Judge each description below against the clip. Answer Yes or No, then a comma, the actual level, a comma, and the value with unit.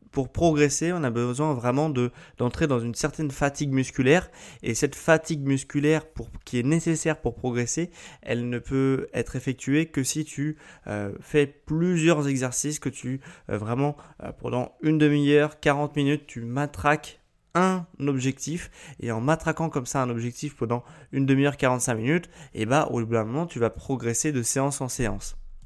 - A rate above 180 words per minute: No, average, 175 wpm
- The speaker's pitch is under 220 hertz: Yes, medium, 140 Hz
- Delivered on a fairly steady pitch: No, average, 3.8 semitones